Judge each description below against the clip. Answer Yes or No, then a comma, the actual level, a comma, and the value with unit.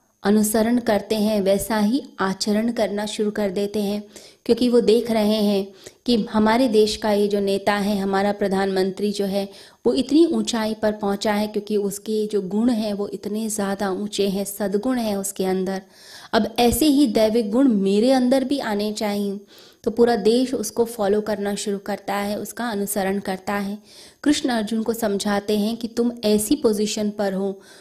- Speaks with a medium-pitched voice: No, high, 210 Hz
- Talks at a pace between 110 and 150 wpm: No, average, 175 wpm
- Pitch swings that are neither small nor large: No, narrow, 2.1 semitones